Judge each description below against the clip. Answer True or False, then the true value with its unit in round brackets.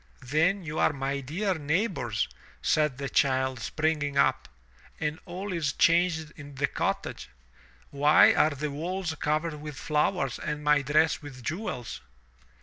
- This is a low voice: False (150 Hz)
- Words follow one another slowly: False (145 wpm)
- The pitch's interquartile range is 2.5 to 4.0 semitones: True (2.8 semitones)